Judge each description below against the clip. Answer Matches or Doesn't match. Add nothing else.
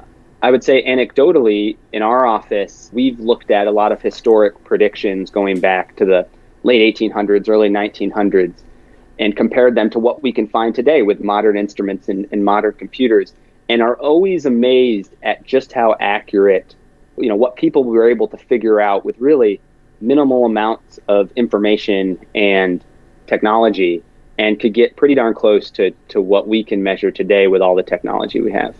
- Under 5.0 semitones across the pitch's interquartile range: Matches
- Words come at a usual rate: Matches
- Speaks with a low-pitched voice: Matches